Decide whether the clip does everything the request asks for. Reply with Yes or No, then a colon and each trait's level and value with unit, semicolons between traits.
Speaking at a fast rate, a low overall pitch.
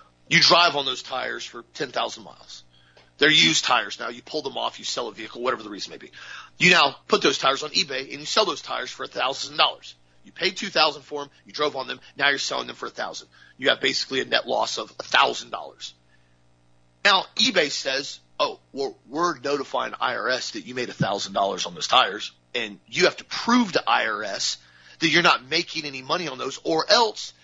Yes: fast, 225 wpm; low, 130 Hz